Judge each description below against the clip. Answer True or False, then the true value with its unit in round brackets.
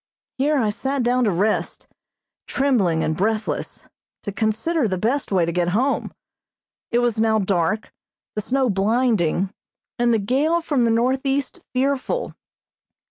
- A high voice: True (230 Hz)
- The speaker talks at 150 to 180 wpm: False (140 wpm)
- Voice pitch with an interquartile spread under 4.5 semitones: False (4.9 semitones)